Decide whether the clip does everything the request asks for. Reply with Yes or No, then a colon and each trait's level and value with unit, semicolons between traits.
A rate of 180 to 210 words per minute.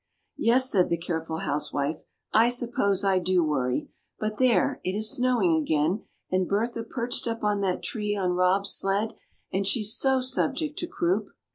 No: average, 170 wpm